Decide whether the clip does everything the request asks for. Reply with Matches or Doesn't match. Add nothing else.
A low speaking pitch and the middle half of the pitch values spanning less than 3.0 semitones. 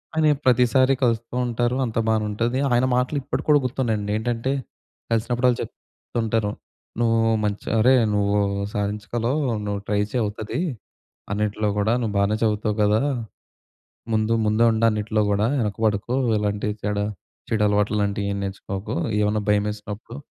Matches